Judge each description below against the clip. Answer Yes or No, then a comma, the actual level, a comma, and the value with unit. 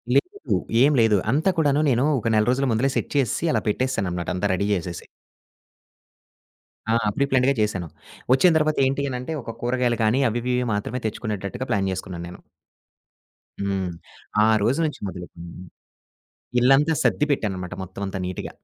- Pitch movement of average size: No, wide, 5.8 semitones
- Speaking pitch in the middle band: No, low, 120 Hz